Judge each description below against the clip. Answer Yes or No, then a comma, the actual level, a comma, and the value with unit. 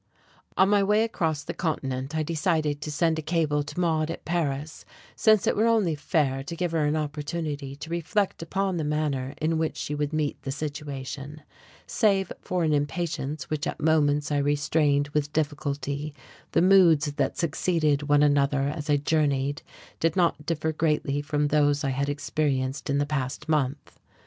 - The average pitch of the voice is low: No, medium, 150 Hz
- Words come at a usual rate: Yes, average, 175 wpm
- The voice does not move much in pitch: Yes, narrow, 2.1 semitones